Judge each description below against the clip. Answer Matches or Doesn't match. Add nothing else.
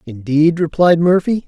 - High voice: Doesn't match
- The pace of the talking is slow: Matches